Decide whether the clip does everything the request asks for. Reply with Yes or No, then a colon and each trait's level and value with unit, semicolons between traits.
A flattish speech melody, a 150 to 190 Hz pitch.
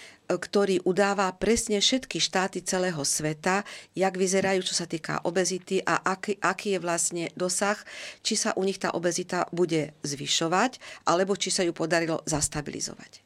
Yes: narrow, 2.3 semitones; medium, 185 Hz